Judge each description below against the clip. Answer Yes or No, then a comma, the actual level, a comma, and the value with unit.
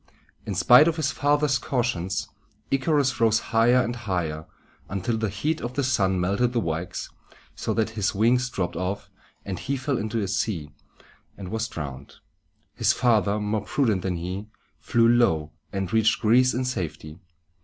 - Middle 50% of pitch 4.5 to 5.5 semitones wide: Yes, average, 4.9 semitones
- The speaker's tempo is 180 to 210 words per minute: No, average, 165 wpm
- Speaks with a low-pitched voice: Yes, low, 110 Hz